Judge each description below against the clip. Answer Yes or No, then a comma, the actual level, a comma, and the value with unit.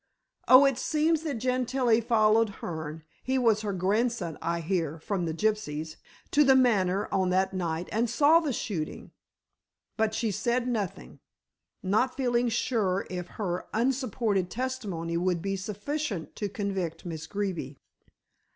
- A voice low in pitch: No, high, 205 Hz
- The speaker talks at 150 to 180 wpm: No, average, 140 wpm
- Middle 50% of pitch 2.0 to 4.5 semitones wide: No, wide, 5.5 semitones